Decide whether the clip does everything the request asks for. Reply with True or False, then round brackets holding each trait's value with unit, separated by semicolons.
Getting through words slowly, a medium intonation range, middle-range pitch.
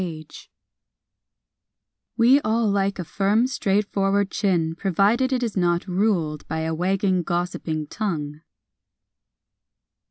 False (105 wpm; 3.7 semitones; 195 Hz)